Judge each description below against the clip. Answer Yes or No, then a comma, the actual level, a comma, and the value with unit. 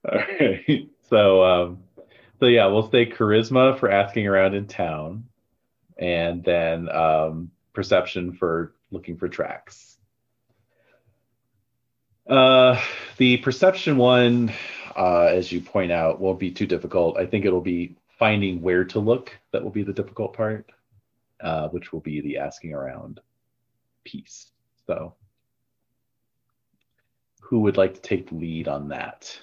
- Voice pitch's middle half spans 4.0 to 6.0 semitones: Yes, average, 5.2 semitones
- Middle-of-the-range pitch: No, low, 105 Hz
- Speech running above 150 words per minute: No, slow, 135 wpm